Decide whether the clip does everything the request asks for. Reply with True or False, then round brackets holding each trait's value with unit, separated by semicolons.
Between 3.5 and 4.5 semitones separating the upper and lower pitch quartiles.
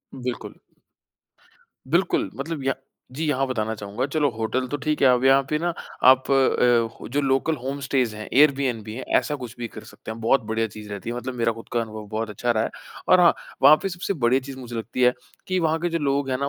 True (3.8 semitones)